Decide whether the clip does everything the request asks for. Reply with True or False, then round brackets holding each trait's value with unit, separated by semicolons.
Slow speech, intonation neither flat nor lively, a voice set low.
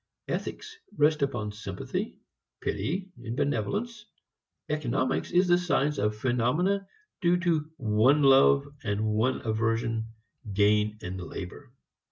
False (110 wpm; 8.1 semitones; 130 Hz)